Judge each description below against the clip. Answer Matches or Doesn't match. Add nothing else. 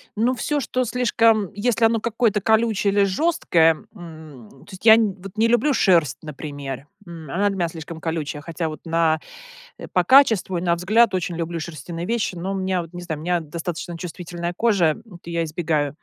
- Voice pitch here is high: Doesn't match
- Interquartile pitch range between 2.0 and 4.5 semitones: Doesn't match